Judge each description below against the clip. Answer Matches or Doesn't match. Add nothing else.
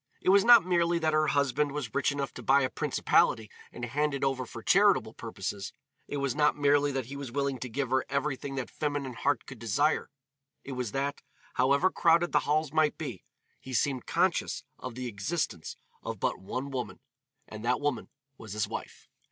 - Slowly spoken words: Doesn't match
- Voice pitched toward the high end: Doesn't match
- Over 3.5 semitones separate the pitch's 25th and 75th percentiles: Doesn't match